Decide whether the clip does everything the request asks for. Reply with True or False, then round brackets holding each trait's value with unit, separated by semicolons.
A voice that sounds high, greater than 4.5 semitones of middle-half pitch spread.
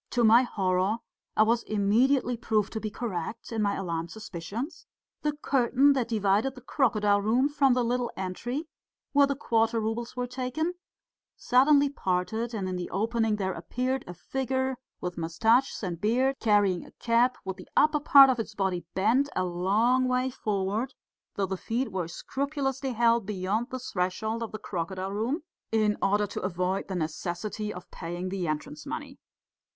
True (220 Hz; 4.9 semitones)